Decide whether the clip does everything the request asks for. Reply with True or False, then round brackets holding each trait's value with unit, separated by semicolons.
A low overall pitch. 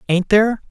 False (205 Hz)